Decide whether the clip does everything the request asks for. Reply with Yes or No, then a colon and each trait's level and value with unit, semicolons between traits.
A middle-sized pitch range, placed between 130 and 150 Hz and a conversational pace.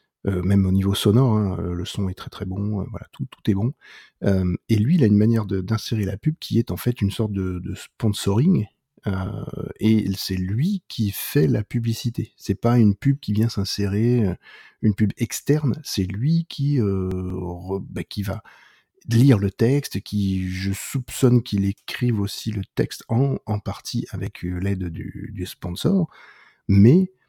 No: average, 3.6 semitones; low, 105 Hz; average, 185 wpm